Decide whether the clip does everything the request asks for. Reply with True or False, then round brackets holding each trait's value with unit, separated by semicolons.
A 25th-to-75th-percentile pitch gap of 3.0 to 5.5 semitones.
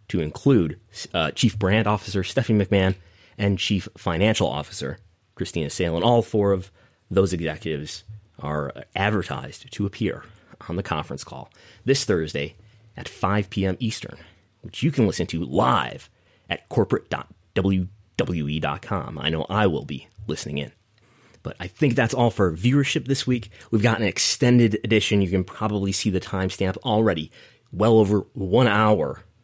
True (3.4 semitones)